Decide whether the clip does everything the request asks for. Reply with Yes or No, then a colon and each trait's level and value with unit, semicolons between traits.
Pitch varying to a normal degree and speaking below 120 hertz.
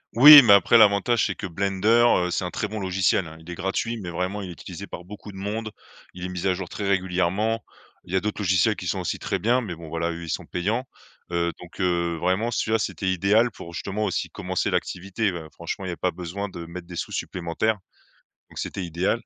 Yes: average, 3.3 semitones; very low, 95 Hz